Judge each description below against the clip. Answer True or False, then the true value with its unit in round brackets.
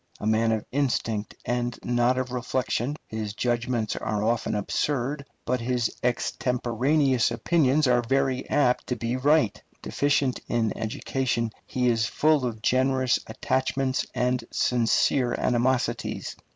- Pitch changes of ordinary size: False (2.1 semitones)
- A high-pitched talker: False (125 Hz)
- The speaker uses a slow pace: True (125 wpm)